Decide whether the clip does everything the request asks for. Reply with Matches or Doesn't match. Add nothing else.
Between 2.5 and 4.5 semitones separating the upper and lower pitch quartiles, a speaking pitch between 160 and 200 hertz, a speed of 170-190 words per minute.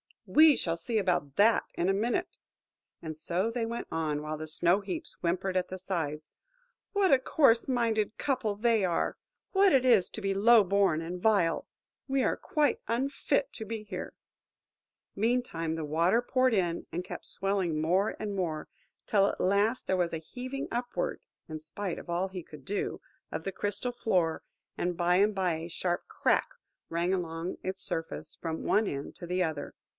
Doesn't match